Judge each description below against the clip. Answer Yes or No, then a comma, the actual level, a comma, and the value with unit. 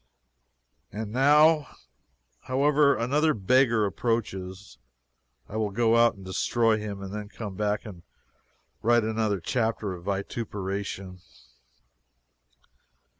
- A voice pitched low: Yes, low, 110 Hz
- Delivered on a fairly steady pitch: No, average, 3.3 semitones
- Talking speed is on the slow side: Yes, slow, 105 wpm